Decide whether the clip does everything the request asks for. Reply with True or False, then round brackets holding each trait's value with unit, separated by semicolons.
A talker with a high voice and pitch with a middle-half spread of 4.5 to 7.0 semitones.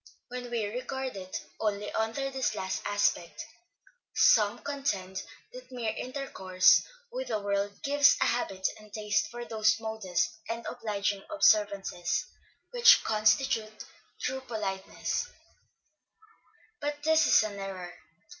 False (220 Hz; 4.1 semitones)